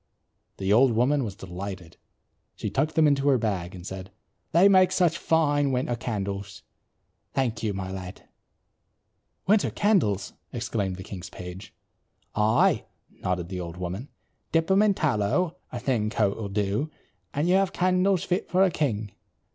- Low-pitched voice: Yes, low, 110 Hz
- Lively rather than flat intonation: Yes, wide, 8.5 semitones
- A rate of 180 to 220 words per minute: No, average, 155 wpm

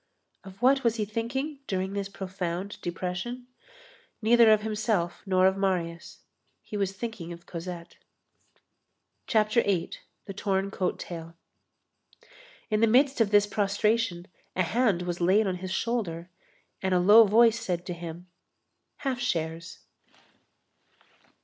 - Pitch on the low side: No, high, 195 Hz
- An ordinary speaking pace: No, slow, 130 wpm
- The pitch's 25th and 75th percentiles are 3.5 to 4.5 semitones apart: Yes, average, 4.0 semitones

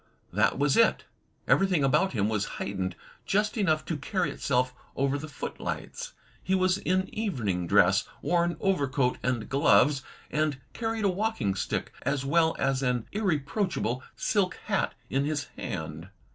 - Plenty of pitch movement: Yes, wide, 6.9 semitones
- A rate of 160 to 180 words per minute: No, average, 150 wpm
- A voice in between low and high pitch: Yes, medium, 145 Hz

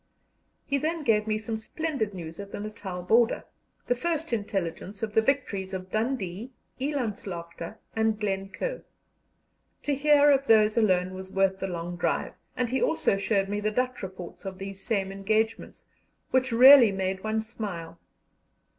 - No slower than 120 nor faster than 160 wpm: Yes, average, 155 wpm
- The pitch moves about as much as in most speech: Yes, average, 4.3 semitones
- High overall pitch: Yes, high, 215 Hz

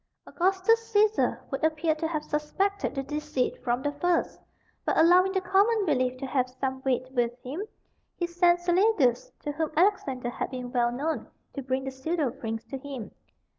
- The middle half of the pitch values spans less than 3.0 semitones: No, wide, 5.4 semitones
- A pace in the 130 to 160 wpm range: No, average, 175 wpm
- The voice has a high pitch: Yes, very high, 295 Hz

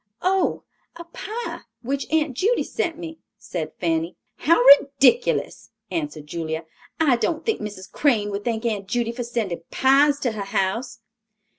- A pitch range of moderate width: No, wide, 7.7 semitones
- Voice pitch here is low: No, high, 245 Hz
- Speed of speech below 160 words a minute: Yes, average, 150 wpm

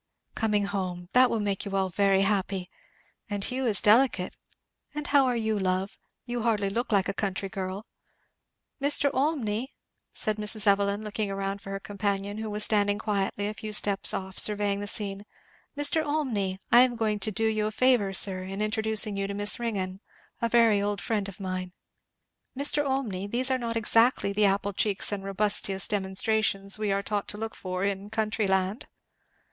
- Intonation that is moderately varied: No, narrow, 2.2 semitones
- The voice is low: No, high, 205 Hz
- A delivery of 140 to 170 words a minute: No, average, 185 wpm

